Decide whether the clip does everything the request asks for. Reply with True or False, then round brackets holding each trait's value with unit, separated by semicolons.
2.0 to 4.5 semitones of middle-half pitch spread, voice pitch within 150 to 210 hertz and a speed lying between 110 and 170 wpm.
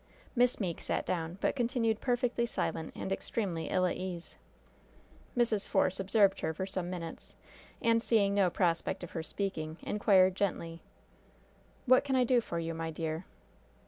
False (5.3 semitones; 190 Hz; 160 wpm)